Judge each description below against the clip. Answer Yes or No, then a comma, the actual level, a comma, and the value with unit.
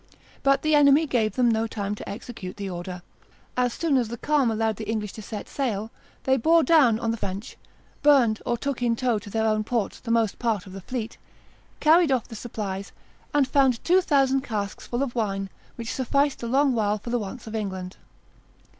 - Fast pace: Yes, fast, 210 wpm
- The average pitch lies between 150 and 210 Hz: No, high, 230 Hz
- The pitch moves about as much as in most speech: Yes, average, 4.0 semitones